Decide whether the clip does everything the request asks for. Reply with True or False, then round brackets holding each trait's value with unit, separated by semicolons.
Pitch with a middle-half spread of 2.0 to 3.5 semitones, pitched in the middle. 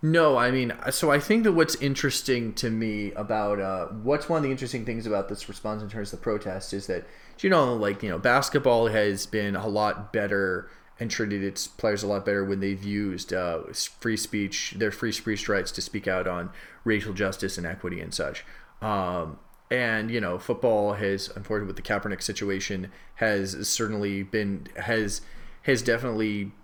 False (2.8 semitones; 105 Hz)